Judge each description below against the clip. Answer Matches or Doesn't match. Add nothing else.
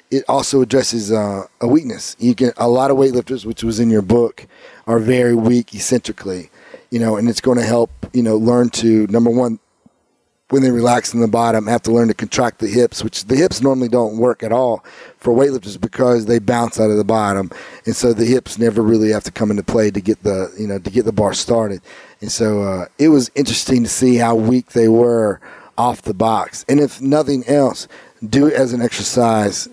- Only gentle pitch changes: Matches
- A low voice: Matches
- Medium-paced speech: Doesn't match